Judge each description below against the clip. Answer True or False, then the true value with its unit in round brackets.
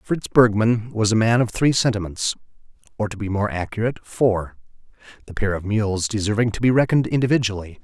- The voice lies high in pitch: False (110 Hz)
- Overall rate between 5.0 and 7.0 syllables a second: True (5.9 syllables/s)